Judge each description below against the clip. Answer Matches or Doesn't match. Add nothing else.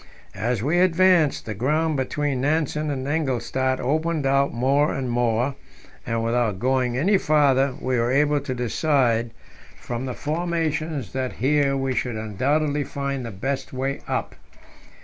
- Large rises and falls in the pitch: Doesn't match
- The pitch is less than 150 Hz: Matches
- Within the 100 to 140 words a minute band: Doesn't match